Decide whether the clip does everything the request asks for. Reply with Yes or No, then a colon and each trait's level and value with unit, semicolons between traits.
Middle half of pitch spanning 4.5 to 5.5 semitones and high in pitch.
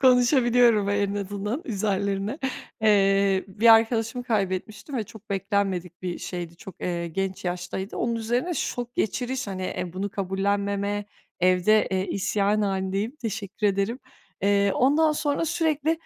No: average, 3.5 semitones; high, 205 Hz